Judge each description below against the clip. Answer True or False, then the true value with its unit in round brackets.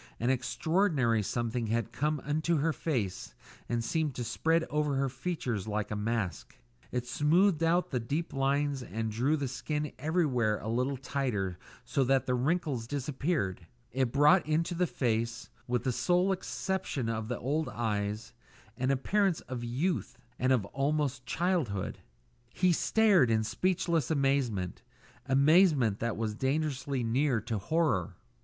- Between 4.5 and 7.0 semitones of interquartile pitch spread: True (5.1 semitones)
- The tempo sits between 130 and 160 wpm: True (150 wpm)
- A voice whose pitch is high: False (135 Hz)